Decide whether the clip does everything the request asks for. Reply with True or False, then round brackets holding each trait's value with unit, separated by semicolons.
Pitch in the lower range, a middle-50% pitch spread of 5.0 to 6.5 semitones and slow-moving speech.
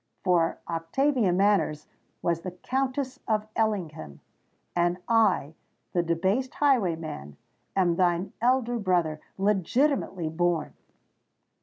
False (185 Hz; 5.4 semitones; 90 wpm)